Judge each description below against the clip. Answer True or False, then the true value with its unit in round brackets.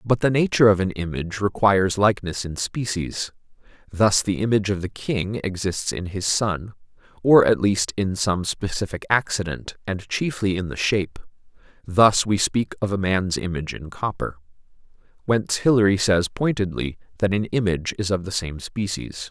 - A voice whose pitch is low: True (100 Hz)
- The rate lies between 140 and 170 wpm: True (165 wpm)